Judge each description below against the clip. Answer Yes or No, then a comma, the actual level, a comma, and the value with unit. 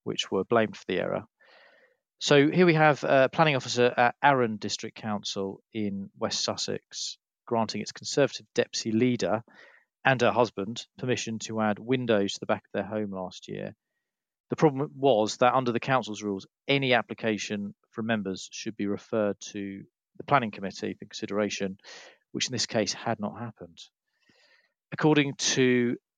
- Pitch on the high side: No, low, 115 Hz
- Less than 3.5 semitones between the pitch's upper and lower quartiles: No, average, 4.0 semitones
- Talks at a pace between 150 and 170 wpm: Yes, average, 160 wpm